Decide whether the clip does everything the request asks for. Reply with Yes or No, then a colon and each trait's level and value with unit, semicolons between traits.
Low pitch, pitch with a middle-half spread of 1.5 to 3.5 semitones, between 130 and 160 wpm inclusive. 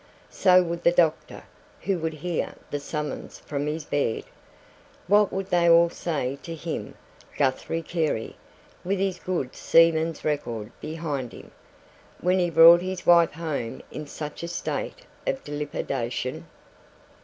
No: medium, 165 Hz; average, 3.0 semitones; average, 140 wpm